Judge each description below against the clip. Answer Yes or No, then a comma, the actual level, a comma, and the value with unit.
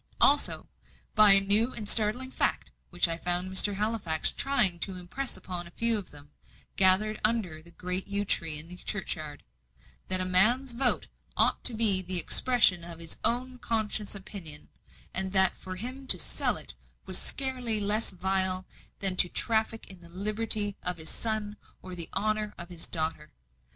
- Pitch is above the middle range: Yes, high, 195 Hz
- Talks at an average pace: Yes, average, 175 wpm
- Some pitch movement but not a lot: Yes, average, 3.5 semitones